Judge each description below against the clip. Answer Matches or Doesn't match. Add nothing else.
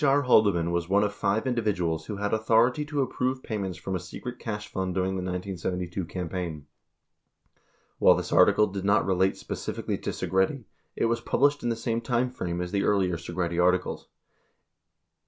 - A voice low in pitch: Matches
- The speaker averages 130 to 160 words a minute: Doesn't match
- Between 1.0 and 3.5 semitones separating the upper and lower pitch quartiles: Doesn't match